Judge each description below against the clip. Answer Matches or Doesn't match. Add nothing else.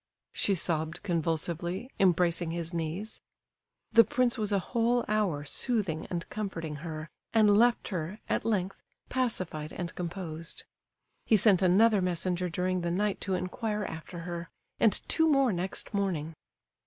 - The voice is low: Doesn't match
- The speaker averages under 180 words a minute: Matches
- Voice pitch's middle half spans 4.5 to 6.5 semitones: Doesn't match